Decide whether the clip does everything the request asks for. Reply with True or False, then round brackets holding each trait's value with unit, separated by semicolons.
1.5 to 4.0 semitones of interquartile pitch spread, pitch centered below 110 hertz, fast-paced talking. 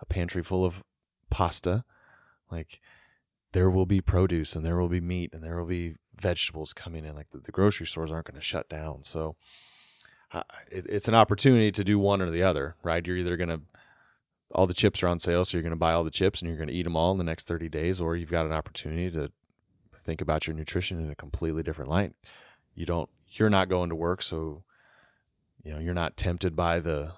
True (2.4 semitones; 85 Hz; 230 wpm)